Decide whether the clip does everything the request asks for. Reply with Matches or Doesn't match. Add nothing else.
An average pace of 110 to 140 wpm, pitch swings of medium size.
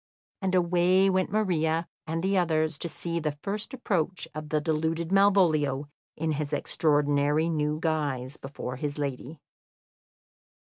Matches